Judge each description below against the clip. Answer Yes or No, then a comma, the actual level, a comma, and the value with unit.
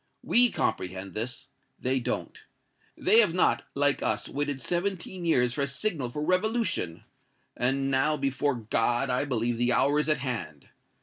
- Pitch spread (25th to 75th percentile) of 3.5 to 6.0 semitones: Yes, average, 5.1 semitones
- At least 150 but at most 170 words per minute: Yes, average, 160 wpm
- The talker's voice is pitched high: No, low, 135 Hz